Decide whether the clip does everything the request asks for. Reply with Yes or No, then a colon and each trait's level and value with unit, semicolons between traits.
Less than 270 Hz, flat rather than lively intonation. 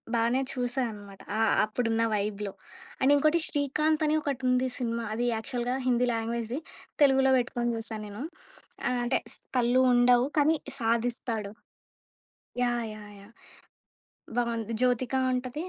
Yes: high, 240 Hz; narrow, 2.1 semitones